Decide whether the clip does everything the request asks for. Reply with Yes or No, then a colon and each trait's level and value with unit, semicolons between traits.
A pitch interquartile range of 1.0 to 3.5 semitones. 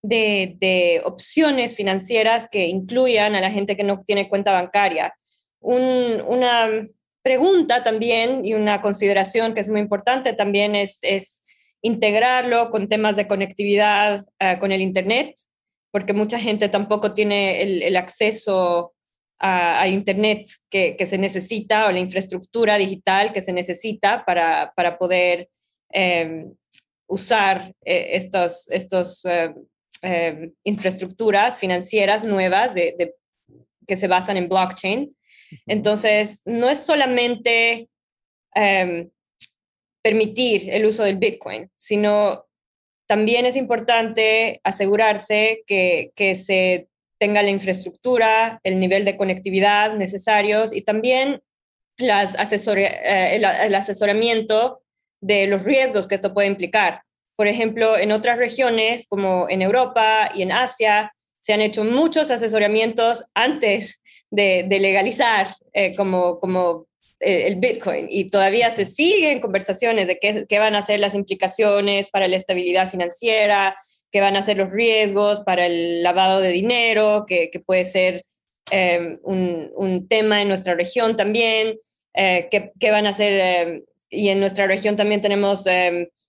Yes: average, 2.7 semitones